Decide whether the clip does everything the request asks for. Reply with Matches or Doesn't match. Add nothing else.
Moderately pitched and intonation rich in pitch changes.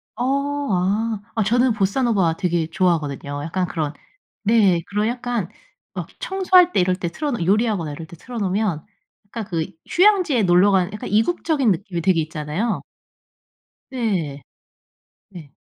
Doesn't match